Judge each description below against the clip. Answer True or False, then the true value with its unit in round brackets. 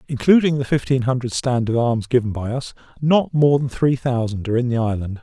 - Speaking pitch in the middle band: False (125 Hz)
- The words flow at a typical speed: False (220 wpm)